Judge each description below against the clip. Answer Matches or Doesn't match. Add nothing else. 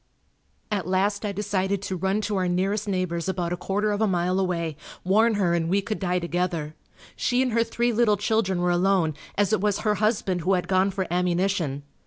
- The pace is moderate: Doesn't match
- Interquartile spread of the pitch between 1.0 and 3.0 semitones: Matches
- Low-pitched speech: Doesn't match